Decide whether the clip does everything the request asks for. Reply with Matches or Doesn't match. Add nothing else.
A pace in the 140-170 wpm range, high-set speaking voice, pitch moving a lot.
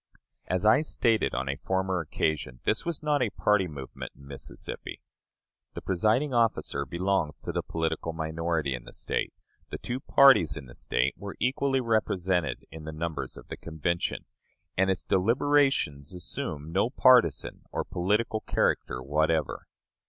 Doesn't match